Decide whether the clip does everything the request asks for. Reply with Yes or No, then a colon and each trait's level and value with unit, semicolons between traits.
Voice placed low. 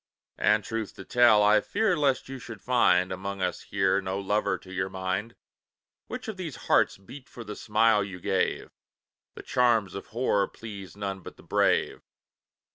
Yes: low, 105 Hz